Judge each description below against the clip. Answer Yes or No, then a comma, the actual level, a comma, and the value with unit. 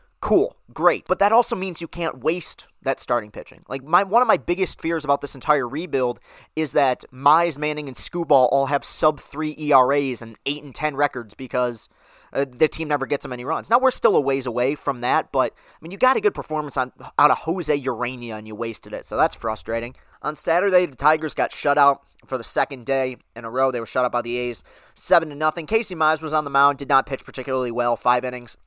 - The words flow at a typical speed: No, fast, 235 wpm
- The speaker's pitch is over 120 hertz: Yes, medium, 140 Hz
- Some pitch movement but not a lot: Yes, average, 3.9 semitones